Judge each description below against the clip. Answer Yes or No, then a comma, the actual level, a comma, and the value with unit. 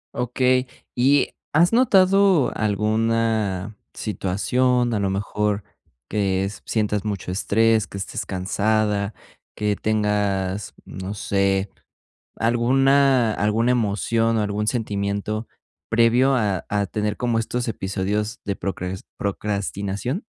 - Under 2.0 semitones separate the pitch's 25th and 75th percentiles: No, average, 2.9 semitones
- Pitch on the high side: No, low, 105 Hz